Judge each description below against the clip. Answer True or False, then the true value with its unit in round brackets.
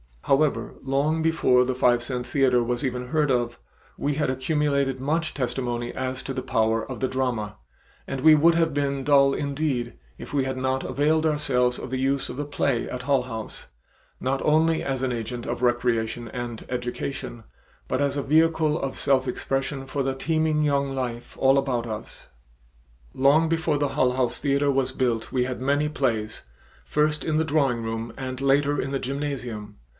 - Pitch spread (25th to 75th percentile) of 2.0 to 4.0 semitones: True (2.6 semitones)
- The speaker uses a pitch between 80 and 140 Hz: True (135 Hz)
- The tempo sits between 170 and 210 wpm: True (180 wpm)